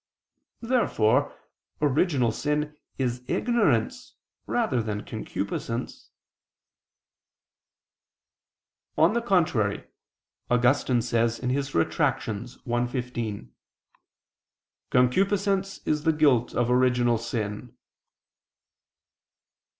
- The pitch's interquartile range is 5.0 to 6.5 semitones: No, average, 4.6 semitones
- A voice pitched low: Yes, low, 125 Hz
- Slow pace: Yes, slow, 70 wpm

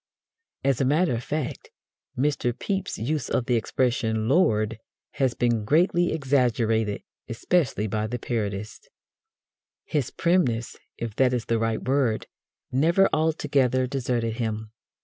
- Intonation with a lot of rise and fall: No, average, 4.2 semitones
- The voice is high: No, low, 125 Hz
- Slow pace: Yes, slow, 130 wpm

